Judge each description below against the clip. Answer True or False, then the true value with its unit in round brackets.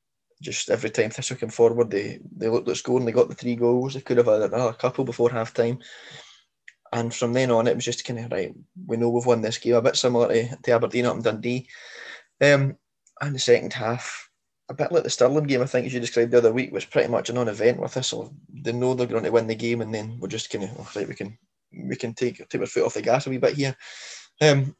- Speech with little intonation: True (2.2 semitones)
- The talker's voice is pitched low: True (125 Hz)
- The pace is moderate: False (255 wpm)